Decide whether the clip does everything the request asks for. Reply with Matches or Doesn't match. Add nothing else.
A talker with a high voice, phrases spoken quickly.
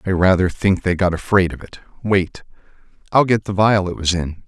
Doesn't match